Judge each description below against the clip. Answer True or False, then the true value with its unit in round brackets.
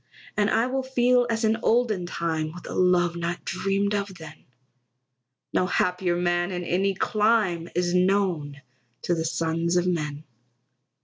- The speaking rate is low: False (150 wpm)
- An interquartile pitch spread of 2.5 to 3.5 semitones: True (3.2 semitones)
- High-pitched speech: False (180 Hz)